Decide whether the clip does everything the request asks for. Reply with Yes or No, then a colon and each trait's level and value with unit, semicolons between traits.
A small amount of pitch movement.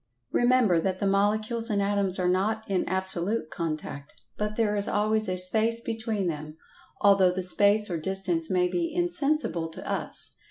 No: average, 3.3 semitones